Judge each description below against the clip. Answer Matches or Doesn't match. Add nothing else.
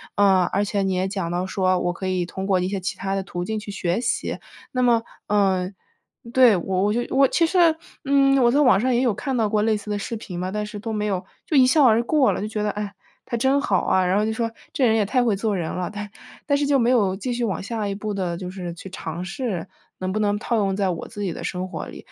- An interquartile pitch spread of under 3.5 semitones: Doesn't match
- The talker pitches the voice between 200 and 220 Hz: Matches